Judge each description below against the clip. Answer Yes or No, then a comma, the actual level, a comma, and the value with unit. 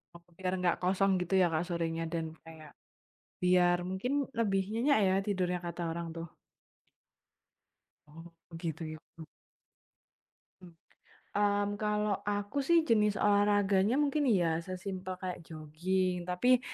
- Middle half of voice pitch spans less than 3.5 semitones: Yes, average, 3.1 semitones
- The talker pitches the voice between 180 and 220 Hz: Yes, medium, 185 Hz